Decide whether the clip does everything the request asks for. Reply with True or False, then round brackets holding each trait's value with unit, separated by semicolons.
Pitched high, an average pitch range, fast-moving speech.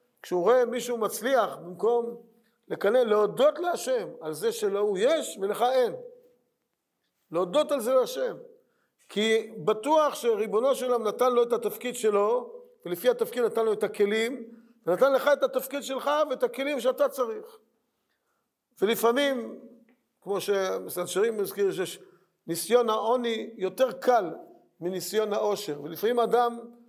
False (245 Hz; 4.9 semitones; 125 wpm)